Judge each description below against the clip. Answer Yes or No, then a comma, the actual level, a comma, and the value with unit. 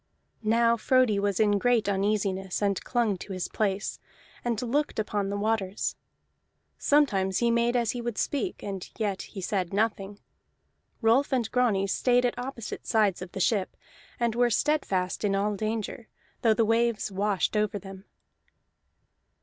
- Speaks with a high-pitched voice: Yes, high, 215 Hz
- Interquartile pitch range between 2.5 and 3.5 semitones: Yes, average, 3.1 semitones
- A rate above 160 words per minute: No, average, 155 wpm